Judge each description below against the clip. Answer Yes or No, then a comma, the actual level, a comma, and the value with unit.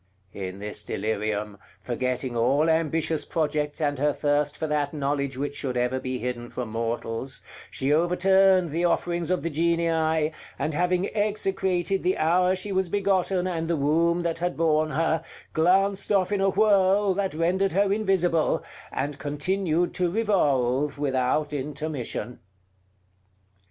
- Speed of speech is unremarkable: Yes, average, 145 wpm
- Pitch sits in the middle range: Yes, medium, 160 Hz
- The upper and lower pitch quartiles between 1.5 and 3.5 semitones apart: No, average, 4.7 semitones